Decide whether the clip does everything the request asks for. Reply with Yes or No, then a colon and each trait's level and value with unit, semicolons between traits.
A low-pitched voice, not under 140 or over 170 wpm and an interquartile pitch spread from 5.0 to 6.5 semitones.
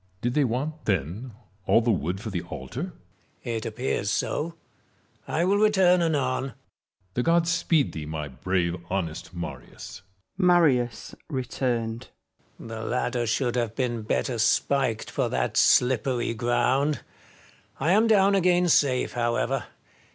Yes: low, 125 Hz; average, 145 wpm; wide, 5.5 semitones